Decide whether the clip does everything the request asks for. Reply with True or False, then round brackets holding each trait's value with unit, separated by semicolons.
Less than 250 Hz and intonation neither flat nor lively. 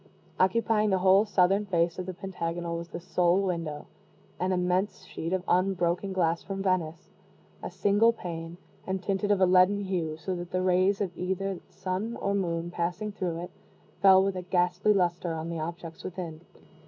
False (185 Hz; 2.1 semitones)